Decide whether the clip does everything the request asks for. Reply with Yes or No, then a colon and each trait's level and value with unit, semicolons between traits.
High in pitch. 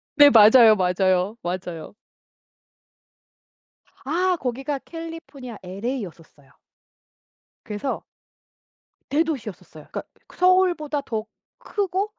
Yes: very high, 250 Hz